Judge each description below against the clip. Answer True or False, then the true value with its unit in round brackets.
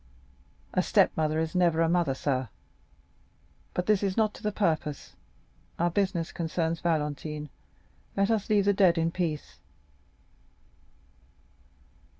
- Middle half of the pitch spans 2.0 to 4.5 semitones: True (3.7 semitones)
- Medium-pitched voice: True (170 Hz)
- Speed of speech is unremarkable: False (120 wpm)